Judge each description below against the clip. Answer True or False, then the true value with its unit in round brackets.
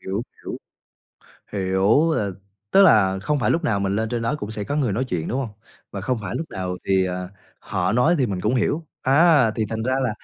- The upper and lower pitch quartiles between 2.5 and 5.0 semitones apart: False (5.6 semitones)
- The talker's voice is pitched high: False (110 Hz)